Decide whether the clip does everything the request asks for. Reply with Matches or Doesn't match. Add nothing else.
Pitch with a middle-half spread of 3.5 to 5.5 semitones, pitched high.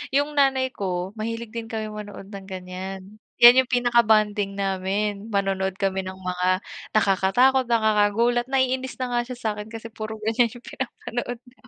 Matches